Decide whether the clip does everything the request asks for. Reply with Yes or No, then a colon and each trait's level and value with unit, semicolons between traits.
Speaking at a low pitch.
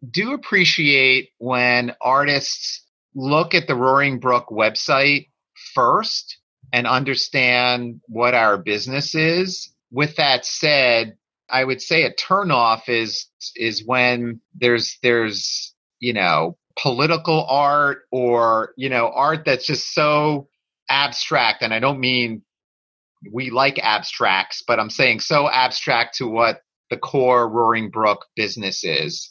Yes: low, 130 Hz